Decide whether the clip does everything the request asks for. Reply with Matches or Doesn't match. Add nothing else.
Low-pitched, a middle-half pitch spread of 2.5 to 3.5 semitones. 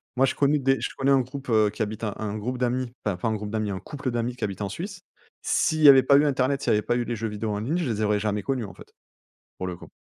Doesn't match